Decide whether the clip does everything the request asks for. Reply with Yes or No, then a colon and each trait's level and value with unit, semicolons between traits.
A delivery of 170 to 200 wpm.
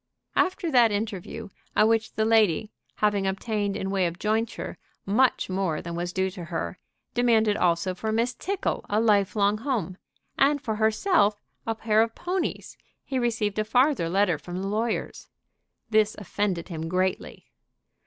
No: average, 160 wpm